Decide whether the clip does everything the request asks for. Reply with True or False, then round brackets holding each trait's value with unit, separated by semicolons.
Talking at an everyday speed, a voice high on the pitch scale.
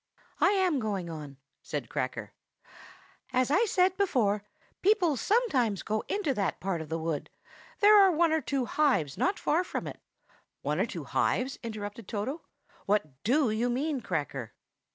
True (160 wpm; 250 Hz)